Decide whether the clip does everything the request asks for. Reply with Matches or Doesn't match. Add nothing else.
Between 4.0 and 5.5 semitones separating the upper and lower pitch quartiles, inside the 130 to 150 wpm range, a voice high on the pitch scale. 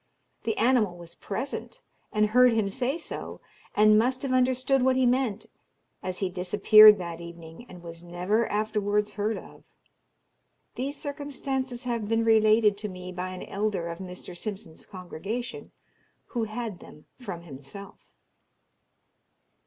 Matches